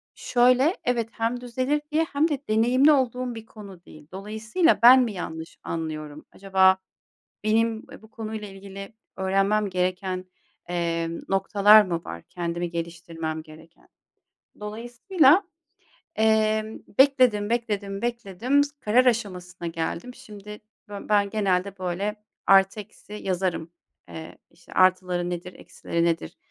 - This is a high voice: Yes, high, 205 Hz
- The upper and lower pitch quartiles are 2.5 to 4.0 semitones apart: No, average, 4.5 semitones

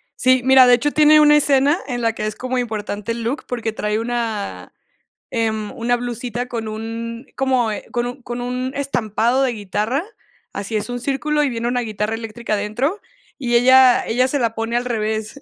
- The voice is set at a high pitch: Yes, high, 240 Hz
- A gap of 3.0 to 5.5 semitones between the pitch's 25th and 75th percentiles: No, narrow, 2.5 semitones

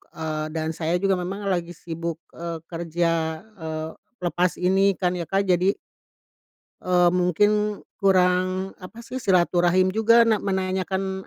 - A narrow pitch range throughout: Yes, narrow, 2.3 semitones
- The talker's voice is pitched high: No, medium, 180 Hz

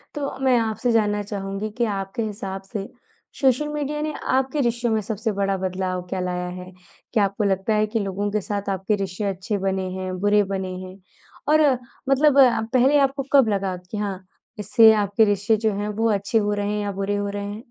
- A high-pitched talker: Yes, high, 205 Hz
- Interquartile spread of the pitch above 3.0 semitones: No, average, 2.7 semitones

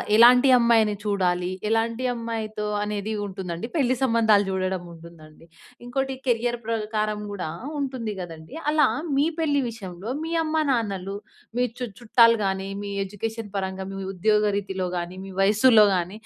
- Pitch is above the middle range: Yes, high, 215 Hz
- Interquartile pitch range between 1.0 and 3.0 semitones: No, average, 3.6 semitones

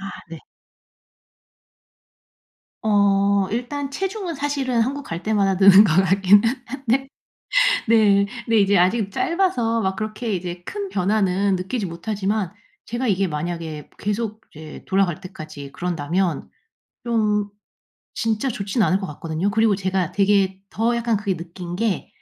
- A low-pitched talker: No, high, 200 Hz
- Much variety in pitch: No, average, 3.8 semitones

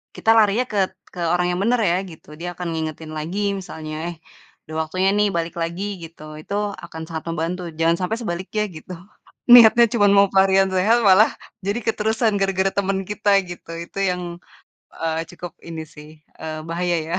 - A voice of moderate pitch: Yes, medium, 180 Hz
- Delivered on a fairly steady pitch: No, average, 3.5 semitones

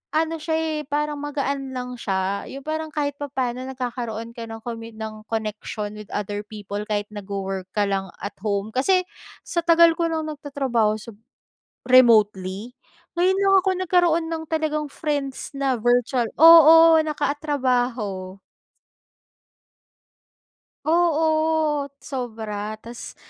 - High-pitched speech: Yes, very high, 255 Hz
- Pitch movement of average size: No, wide, 6.2 semitones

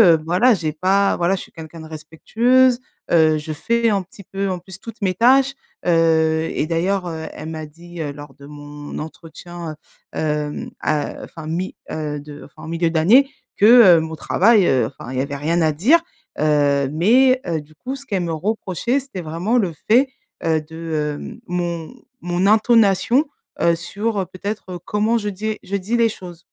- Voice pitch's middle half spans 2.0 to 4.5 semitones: No, average, 4.9 semitones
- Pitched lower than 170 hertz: No, medium, 175 Hz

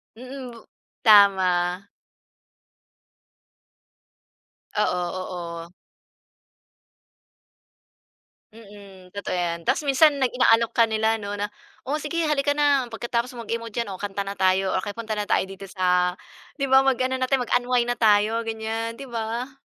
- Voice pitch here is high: Yes, high, 225 Hz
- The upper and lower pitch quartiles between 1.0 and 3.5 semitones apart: No, average, 4.1 semitones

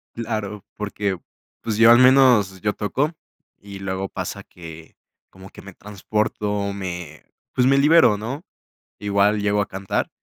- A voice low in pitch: Yes, low, 105 Hz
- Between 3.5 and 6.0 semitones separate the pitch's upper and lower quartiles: No, average, 2.8 semitones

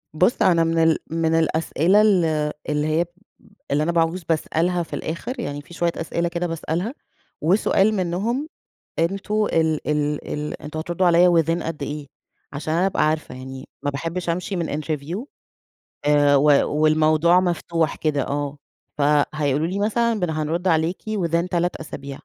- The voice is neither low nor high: Yes, medium, 165 Hz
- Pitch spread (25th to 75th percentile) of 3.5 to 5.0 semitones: No, average, 2.8 semitones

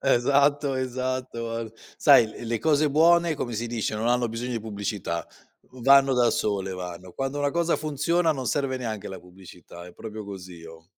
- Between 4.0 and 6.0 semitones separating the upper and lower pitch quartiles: Yes, average, 5.2 semitones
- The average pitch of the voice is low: Yes, low, 120 Hz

